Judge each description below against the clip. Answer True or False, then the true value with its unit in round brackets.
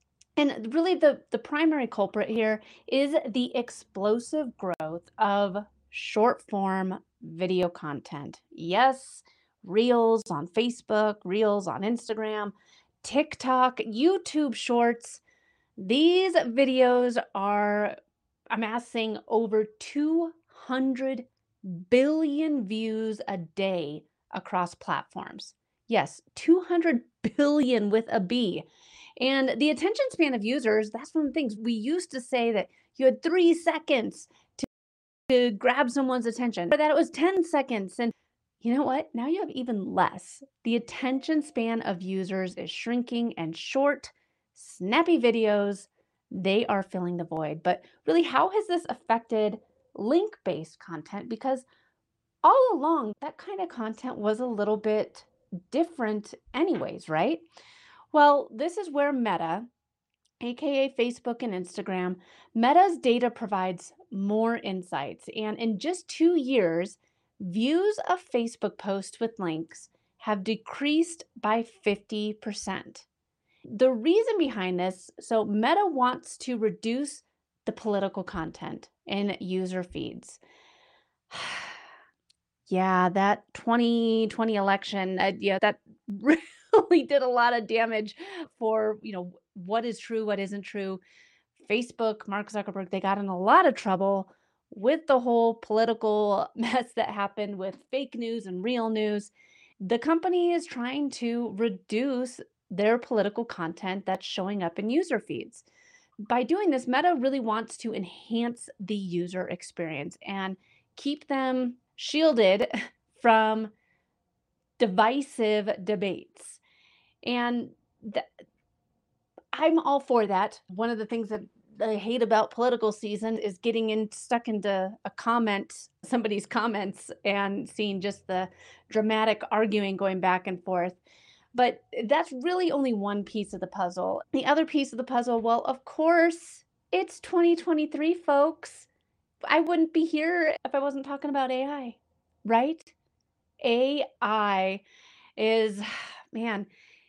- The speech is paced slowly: True (130 wpm)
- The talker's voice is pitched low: False (230 Hz)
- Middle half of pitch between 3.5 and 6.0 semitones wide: True (5.3 semitones)